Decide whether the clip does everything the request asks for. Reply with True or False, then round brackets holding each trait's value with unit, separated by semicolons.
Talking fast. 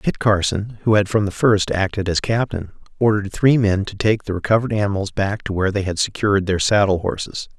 True (215 wpm)